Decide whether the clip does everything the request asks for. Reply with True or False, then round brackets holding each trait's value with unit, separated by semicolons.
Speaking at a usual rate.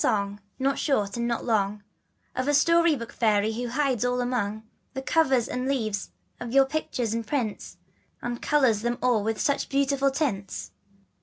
True (160 wpm)